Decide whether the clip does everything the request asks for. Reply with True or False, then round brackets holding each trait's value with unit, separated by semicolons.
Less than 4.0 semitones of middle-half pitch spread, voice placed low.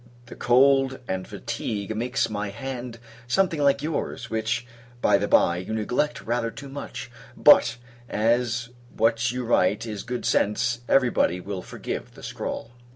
True (2.8 semitones; 120 Hz)